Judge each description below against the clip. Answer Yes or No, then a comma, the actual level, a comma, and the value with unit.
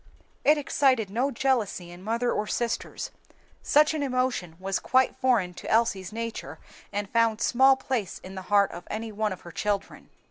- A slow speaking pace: No, average, 175 wpm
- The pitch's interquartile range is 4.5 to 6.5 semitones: Yes, average, 4.8 semitones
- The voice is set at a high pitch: Yes, high, 225 Hz